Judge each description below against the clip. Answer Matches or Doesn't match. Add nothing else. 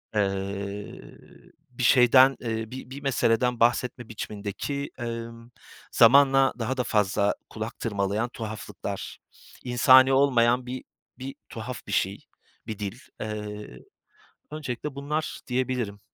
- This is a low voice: Matches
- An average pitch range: Matches